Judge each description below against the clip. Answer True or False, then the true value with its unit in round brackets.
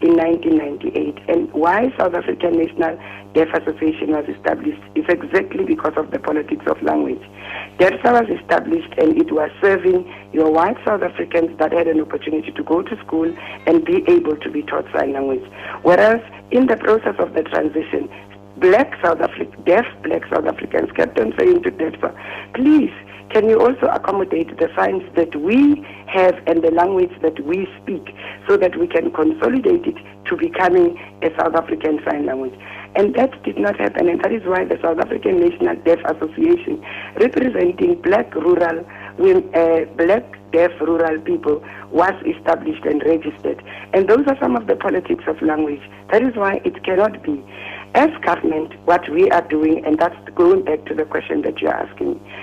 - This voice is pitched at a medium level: True (175 Hz)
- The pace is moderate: True (175 wpm)